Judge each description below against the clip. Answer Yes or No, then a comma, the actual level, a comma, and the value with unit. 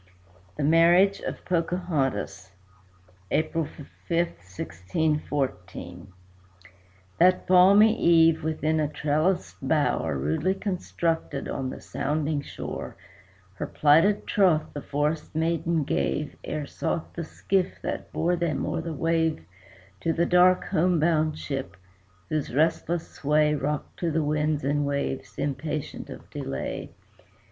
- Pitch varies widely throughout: No, average, 3.0 semitones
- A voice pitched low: No, medium, 155 Hz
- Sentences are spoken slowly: Yes, slow, 120 wpm